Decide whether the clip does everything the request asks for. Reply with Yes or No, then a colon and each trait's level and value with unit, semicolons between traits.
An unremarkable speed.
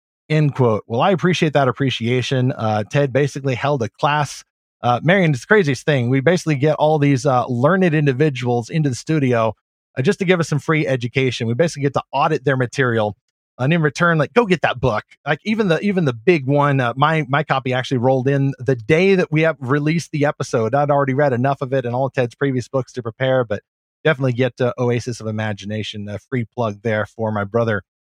No: fast, 225 wpm